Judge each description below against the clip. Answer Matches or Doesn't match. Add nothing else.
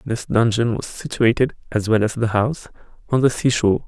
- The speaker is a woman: Doesn't match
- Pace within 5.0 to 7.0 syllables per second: Matches